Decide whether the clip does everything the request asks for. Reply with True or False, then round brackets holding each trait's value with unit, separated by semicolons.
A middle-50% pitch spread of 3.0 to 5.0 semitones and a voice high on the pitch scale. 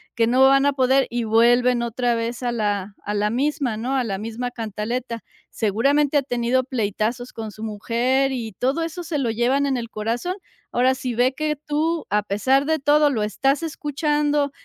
True (3.5 semitones; 245 Hz)